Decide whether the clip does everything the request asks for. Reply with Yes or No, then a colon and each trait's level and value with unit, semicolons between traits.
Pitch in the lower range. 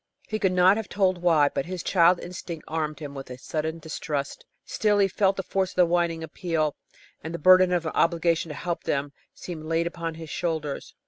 No: medium, 170 Hz